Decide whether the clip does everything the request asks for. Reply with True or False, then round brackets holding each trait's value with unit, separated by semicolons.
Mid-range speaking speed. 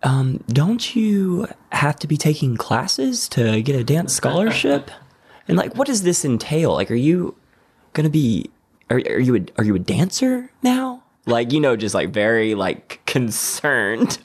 True (175 wpm)